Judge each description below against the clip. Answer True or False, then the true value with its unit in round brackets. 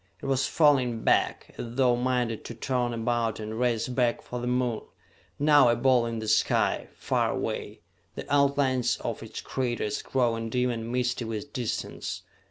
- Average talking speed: True (170 wpm)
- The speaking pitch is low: True (120 Hz)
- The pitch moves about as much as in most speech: False (1.8 semitones)